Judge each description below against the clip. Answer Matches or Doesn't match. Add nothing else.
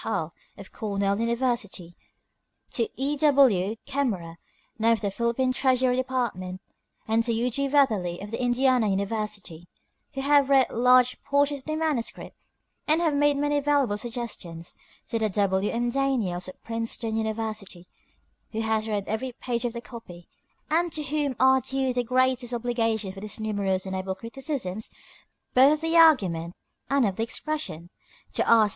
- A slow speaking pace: Doesn't match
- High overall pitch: Matches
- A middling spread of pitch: Matches